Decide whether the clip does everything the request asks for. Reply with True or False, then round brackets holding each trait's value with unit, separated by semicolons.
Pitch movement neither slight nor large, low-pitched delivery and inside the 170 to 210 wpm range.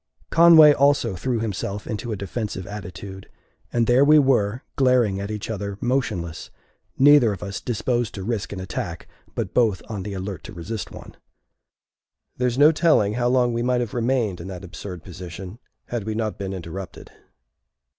True (4.2 semitones; 110 Hz; 175 wpm)